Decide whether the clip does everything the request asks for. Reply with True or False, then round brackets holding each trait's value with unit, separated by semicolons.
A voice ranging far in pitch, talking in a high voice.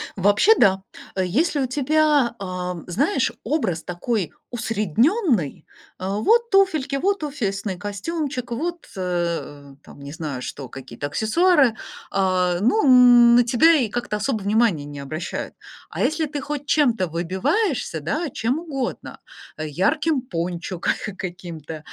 True (8.5 semitones; 220 Hz)